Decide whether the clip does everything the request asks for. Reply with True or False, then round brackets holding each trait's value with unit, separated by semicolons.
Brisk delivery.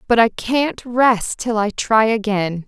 False (180 wpm)